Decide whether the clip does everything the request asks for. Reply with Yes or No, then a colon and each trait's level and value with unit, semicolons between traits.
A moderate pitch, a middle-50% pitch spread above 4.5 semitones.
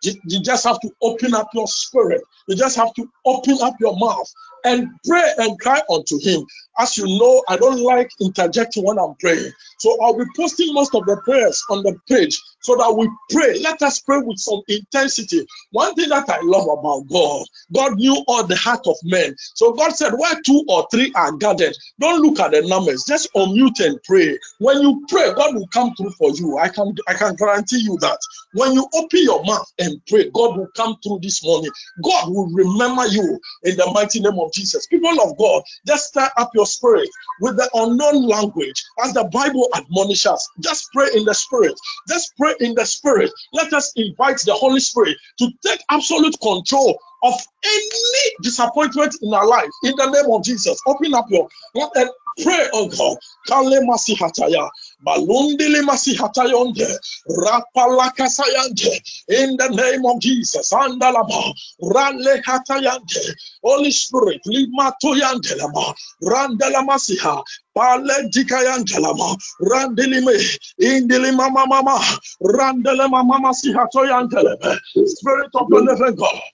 No: very high, 260 Hz; average, 4.9 semitones